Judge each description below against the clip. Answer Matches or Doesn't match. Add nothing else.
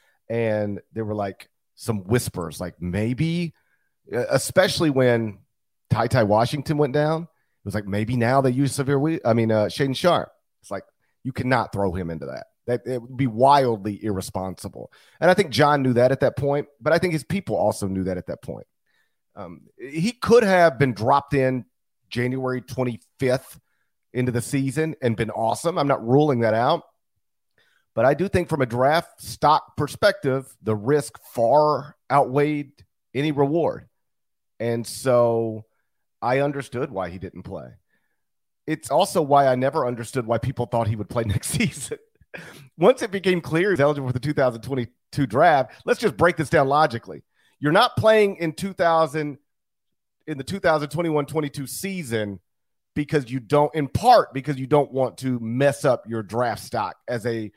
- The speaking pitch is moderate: Doesn't match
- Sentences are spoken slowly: Doesn't match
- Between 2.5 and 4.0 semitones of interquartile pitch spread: Doesn't match